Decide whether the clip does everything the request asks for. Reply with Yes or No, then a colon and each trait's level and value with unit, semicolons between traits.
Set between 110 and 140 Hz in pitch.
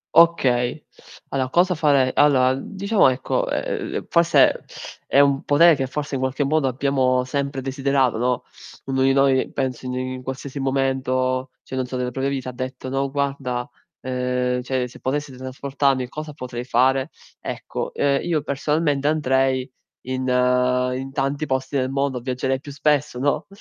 Yes: low, 135 Hz